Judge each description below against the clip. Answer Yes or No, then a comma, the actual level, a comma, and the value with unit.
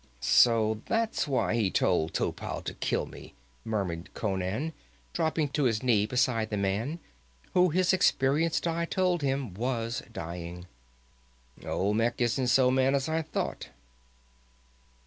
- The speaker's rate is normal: No, slow, 130 wpm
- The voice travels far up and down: Yes, wide, 6.2 semitones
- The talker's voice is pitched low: Yes, low, 125 Hz